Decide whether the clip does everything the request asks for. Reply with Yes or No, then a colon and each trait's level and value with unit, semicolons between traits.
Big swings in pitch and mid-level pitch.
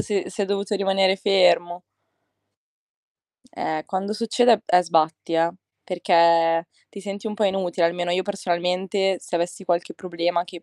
No: narrow, 2.4 semitones; medium, 180 Hz